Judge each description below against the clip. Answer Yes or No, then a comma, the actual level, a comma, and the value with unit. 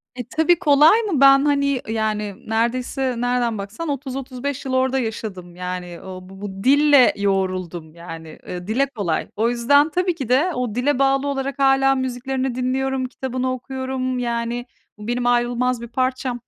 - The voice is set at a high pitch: Yes, very high, 250 Hz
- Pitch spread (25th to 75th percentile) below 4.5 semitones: Yes, average, 3.7 semitones